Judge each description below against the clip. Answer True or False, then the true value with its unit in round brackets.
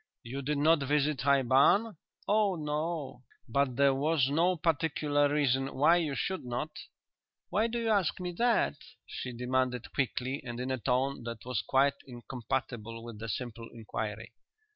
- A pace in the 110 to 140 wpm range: False (160 wpm)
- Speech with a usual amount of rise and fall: True (3.9 semitones)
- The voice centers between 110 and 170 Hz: True (140 Hz)